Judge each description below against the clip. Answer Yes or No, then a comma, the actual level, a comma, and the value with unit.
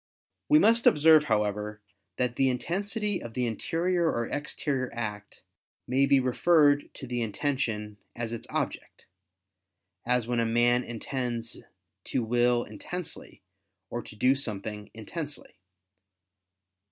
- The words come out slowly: Yes, slow, 125 wpm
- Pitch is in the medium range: No, low, 125 Hz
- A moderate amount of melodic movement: Yes, average, 4.2 semitones